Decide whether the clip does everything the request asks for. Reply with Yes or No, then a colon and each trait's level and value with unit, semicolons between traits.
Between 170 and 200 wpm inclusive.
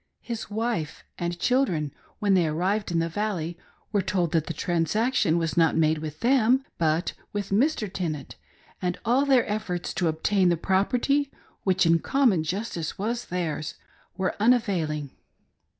No: average, 150 wpm